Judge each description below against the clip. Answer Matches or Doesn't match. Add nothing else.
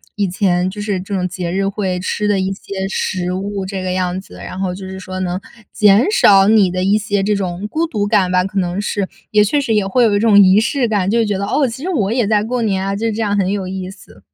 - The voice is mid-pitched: Doesn't match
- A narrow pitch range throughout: Matches